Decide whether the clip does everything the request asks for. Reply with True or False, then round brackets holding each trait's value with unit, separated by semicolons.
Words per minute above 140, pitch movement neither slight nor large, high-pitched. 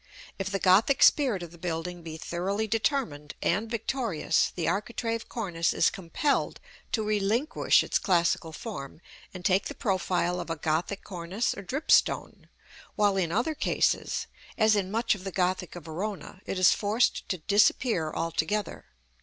True (155 wpm; 4.2 semitones; 195 Hz)